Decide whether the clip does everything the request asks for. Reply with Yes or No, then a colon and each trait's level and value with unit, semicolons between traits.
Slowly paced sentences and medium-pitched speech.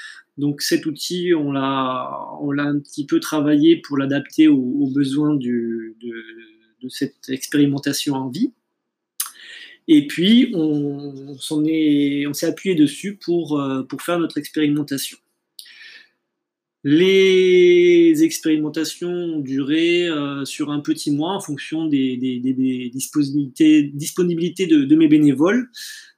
Yes: slow, 130 wpm; medium, 155 Hz